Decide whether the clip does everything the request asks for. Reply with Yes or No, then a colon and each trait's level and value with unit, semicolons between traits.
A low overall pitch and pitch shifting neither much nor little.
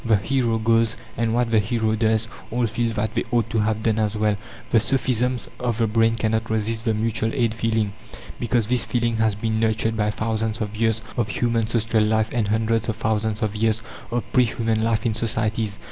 No: low, 110 Hz; narrow, 1.0 semitones